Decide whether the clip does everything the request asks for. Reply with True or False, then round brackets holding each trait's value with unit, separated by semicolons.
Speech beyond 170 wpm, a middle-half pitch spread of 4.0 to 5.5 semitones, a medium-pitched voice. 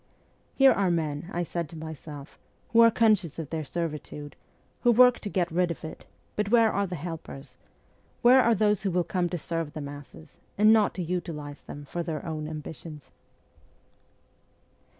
True (180 wpm; 4.8 semitones; 170 Hz)